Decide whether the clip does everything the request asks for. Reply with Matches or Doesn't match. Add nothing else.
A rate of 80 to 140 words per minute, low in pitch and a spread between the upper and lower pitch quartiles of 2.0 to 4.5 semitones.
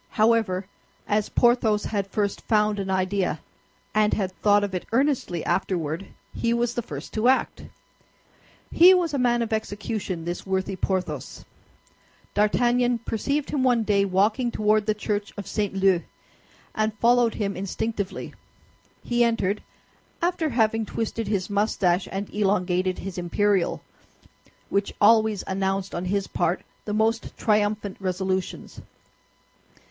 Doesn't match